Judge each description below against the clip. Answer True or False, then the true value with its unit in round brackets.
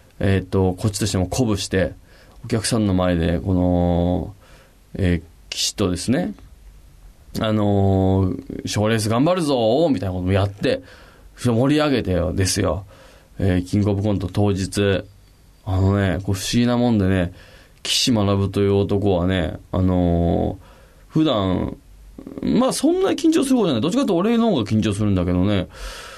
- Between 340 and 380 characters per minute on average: False (315 characters per minute)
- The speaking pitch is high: False (100 Hz)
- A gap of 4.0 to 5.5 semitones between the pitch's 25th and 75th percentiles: False (3.3 semitones)